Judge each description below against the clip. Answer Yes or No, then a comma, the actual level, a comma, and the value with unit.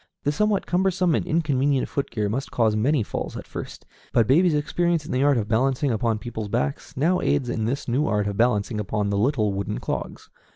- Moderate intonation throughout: No, wide, 5.7 semitones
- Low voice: Yes, low, 125 Hz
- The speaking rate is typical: No, fast, 210 wpm